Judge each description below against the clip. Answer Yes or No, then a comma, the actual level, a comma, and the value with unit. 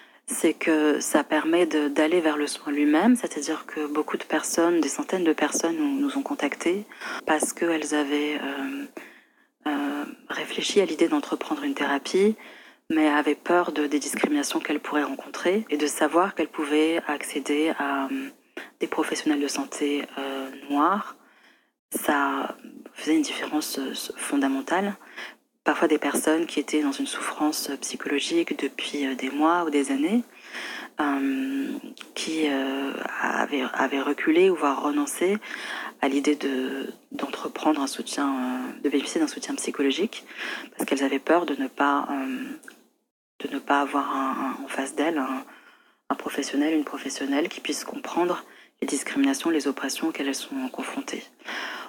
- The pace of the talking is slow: Yes, slow, 140 wpm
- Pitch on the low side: No, medium, 155 Hz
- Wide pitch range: Yes, wide, 6.3 semitones